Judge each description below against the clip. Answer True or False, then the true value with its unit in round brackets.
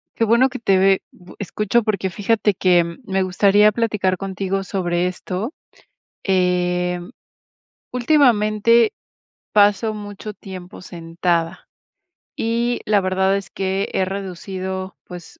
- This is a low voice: False (195 Hz)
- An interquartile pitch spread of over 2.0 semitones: True (2.5 semitones)